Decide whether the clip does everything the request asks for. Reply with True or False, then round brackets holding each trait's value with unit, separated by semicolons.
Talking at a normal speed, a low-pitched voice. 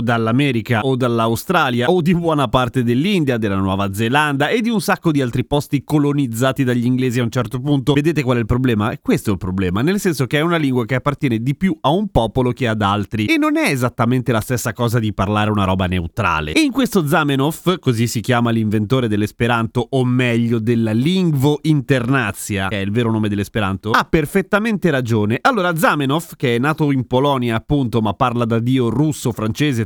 False (200 wpm; 125 Hz)